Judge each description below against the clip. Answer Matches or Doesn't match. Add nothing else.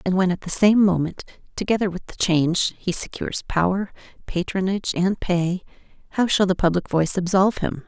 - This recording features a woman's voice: Matches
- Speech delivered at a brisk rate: Doesn't match